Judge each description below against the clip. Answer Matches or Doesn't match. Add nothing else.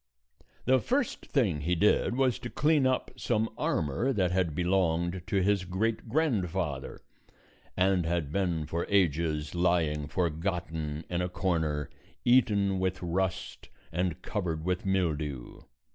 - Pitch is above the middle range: Doesn't match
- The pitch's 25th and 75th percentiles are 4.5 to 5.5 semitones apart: Doesn't match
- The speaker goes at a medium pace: Doesn't match